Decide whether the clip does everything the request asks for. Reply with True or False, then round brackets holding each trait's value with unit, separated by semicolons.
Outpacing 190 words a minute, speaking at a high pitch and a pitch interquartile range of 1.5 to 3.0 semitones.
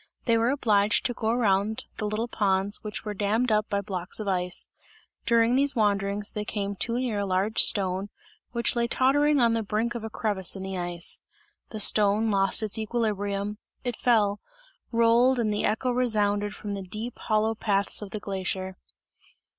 False (180 wpm; 210 Hz; 2.5 semitones)